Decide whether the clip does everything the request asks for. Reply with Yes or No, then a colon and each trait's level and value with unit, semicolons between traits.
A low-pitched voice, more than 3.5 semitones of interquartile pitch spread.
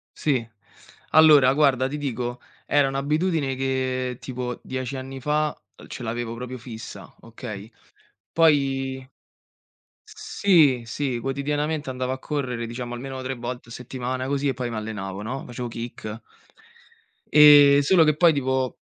No: low, 130 Hz; average, 2.8 semitones